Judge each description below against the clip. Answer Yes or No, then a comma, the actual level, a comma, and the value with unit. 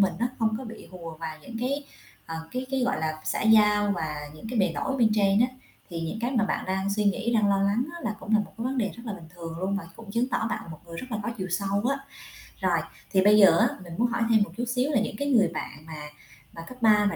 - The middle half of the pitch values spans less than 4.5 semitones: Yes, average, 4.1 semitones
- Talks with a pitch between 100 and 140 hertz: No, high, 210 Hz